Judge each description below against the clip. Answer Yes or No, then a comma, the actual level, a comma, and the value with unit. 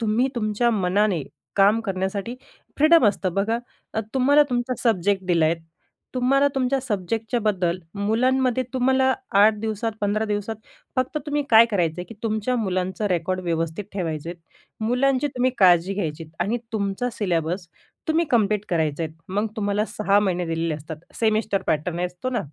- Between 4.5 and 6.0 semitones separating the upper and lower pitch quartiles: Yes, average, 4.8 semitones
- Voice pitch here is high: Yes, high, 210 Hz